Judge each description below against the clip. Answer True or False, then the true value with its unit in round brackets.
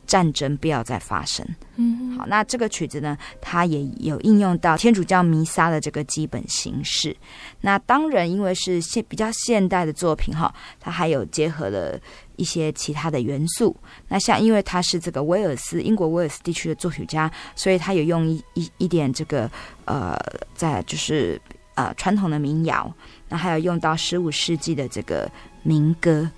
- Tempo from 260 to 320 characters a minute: True (270 characters per minute)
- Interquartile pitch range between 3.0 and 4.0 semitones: True (3.3 semitones)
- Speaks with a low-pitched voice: False (165 Hz)